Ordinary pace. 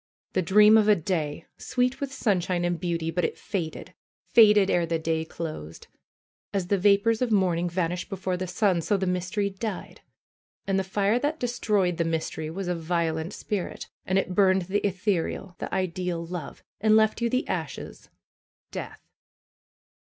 Yes: average, 170 wpm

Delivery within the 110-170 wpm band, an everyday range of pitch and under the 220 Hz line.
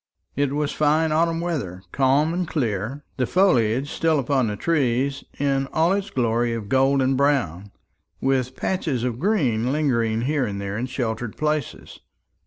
Yes: average, 160 wpm; average, 4.6 semitones; low, 135 Hz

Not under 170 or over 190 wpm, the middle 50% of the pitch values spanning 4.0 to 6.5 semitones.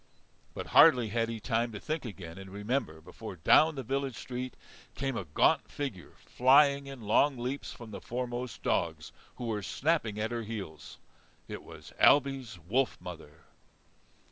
No: average, 160 wpm; average, 4.7 semitones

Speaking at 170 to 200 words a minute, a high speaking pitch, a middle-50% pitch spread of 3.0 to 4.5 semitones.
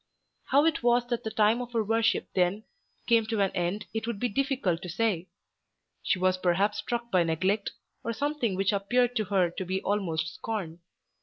Yes: average, 190 wpm; high, 210 Hz; average, 4.2 semitones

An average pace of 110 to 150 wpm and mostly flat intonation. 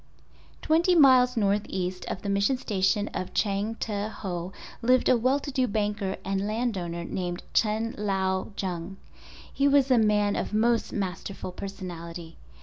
No: average, 140 wpm; average, 3.7 semitones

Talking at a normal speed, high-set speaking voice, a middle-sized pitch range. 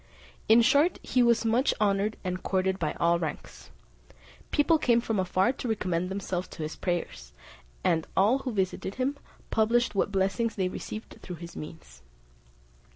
Yes: average, 155 wpm; high, 195 Hz; average, 4.7 semitones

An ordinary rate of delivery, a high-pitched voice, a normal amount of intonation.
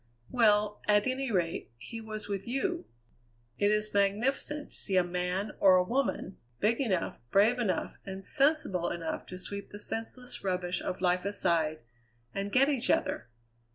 Yes: average, 160 wpm; high, 205 Hz; average, 4.1 semitones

